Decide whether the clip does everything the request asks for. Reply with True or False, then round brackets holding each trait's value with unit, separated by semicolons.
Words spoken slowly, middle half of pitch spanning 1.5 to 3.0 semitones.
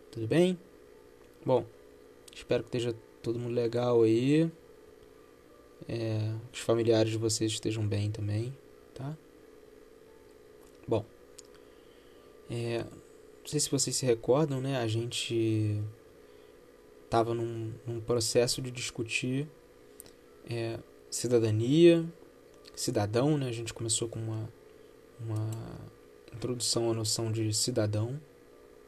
True (105 wpm; 2.4 semitones)